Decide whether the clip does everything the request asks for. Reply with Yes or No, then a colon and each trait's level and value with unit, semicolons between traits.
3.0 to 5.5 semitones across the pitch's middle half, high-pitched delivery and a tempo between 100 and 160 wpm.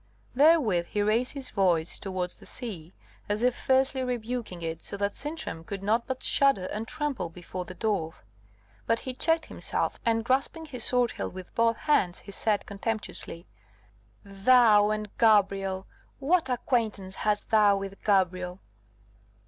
Yes: average, 4.7 semitones; high, 215 Hz; average, 150 wpm